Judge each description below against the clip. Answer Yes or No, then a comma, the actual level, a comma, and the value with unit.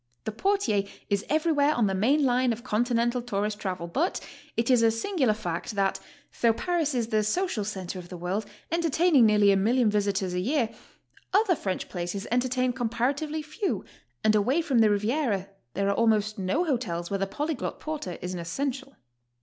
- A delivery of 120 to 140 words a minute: No, average, 180 wpm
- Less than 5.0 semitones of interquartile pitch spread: No, wide, 5.6 semitones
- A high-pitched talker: Yes, high, 230 Hz